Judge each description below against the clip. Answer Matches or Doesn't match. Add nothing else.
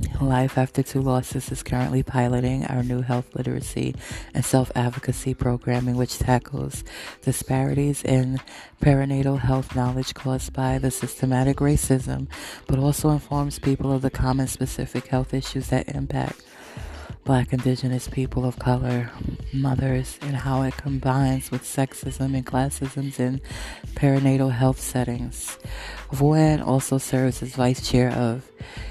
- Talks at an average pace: Doesn't match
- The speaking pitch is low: Matches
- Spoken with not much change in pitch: Matches